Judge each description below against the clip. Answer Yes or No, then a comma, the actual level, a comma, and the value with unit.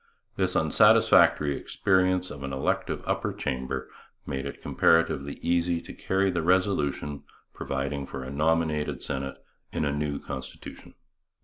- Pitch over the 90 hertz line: No, very low, 75 Hz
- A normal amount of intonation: Yes, average, 3.6 semitones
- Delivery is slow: Yes, slow, 130 wpm